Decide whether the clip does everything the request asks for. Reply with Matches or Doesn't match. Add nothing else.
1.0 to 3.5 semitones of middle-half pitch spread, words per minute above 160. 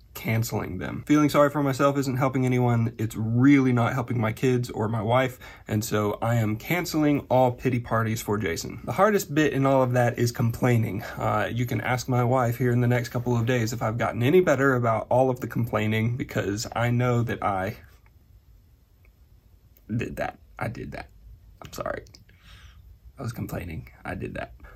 Matches